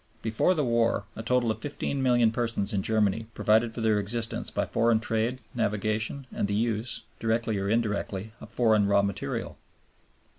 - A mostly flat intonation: Yes, narrow, 1.9 semitones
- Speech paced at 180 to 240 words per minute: No, average, 170 wpm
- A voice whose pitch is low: Yes, low, 110 Hz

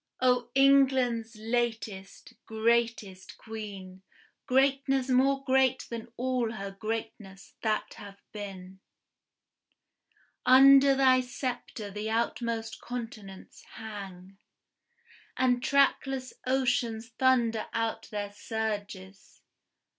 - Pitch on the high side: Yes, high, 230 Hz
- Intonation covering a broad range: No, average, 3.6 semitones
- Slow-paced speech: Yes, slow, 85 wpm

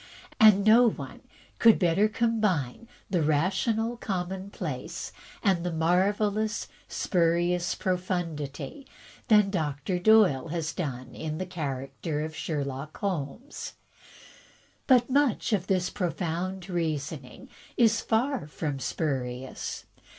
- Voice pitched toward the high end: No, medium, 180 Hz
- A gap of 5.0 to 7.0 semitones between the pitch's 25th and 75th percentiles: Yes, wide, 5.5 semitones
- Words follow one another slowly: Yes, slow, 105 wpm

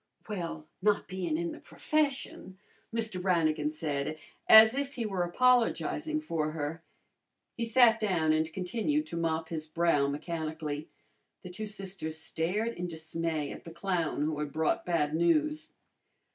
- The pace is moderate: Yes, average, 145 wpm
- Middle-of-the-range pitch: Yes, medium, 170 Hz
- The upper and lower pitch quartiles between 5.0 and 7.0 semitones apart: Yes, wide, 5.6 semitones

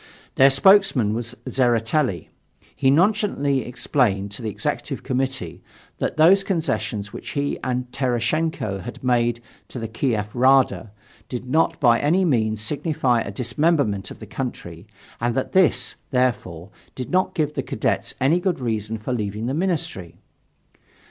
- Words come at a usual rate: Yes, average, 145 wpm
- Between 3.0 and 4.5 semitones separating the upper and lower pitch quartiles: No, average, 4.9 semitones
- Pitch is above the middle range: No, low, 125 Hz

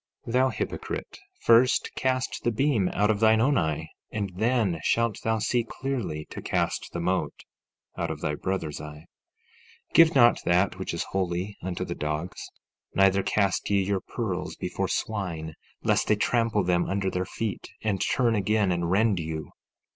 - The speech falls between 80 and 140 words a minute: No, average, 170 wpm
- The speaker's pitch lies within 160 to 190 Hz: No, low, 100 Hz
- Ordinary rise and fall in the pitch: Yes, average, 4.4 semitones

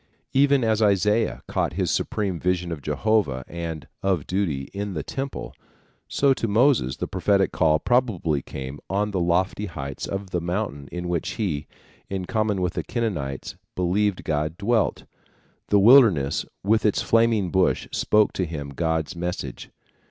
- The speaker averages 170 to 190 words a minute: No, average, 155 wpm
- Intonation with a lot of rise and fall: No, average, 4.7 semitones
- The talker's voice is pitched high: No, very low, 95 Hz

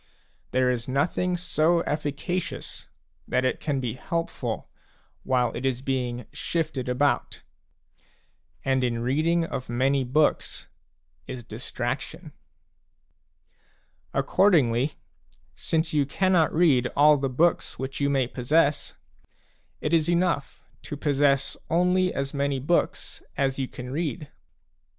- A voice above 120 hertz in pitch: Yes, medium, 140 Hz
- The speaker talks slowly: Yes, slow, 120 wpm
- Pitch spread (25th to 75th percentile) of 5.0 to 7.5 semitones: No, average, 4.1 semitones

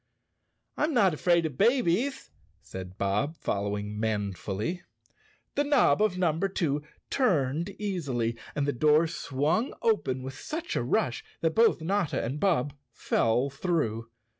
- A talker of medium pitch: Yes, medium, 150 Hz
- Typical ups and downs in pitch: No, wide, 8.2 semitones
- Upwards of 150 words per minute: No, average, 140 wpm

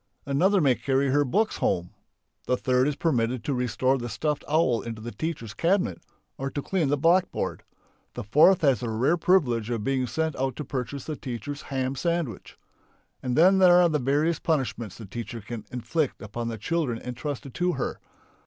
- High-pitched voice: No, low, 135 Hz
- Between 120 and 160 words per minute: No, average, 185 wpm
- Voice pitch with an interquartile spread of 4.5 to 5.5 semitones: Yes, average, 5.0 semitones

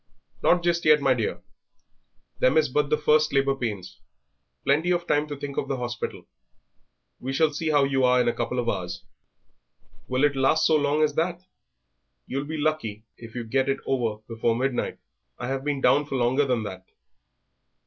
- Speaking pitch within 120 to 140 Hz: Yes, low, 135 Hz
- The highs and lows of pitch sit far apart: No, average, 3.5 semitones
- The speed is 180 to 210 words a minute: Yes, average, 190 wpm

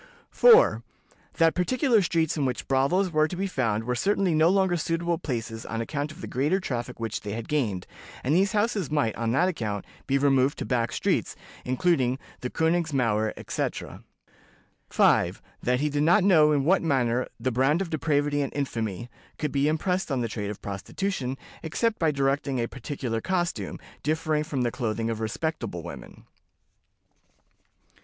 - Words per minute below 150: No, average, 170 wpm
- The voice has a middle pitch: Yes, medium, 145 Hz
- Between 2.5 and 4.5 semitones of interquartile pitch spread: No, wide, 5.6 semitones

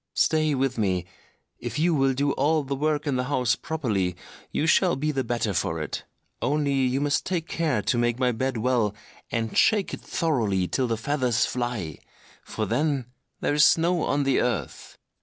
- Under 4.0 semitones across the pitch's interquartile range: No, average, 4.4 semitones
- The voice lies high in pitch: No, low, 130 Hz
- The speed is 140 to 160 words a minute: No, average, 180 wpm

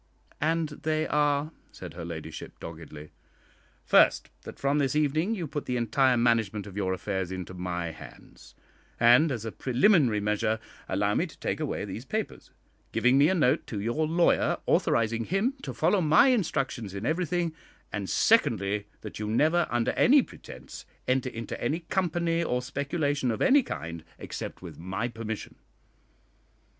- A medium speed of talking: Yes, average, 160 wpm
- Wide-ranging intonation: Yes, wide, 7.2 semitones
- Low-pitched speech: Yes, low, 125 Hz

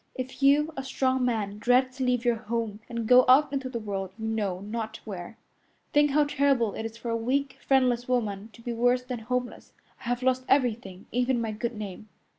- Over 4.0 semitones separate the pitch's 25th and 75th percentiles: No, average, 2.8 semitones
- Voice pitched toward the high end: Yes, high, 240 Hz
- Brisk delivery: Yes, fast, 210 wpm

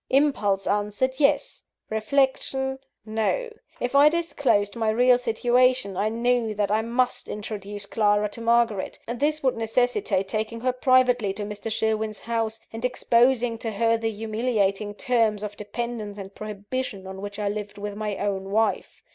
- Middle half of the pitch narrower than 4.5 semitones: Yes, average, 3.1 semitones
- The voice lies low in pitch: No, high, 225 Hz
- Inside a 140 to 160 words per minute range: Yes, average, 155 wpm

